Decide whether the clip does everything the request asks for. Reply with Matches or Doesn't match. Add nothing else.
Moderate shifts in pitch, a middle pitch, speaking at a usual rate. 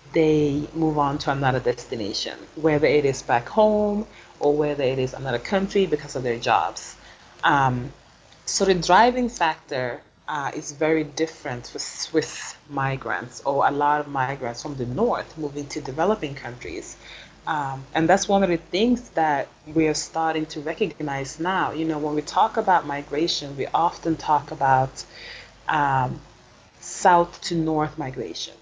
Matches